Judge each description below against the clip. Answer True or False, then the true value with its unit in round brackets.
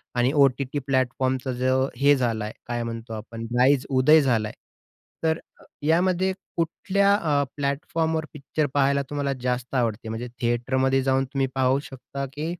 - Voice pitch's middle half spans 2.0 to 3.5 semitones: True (2.8 semitones)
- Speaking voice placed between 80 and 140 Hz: True (135 Hz)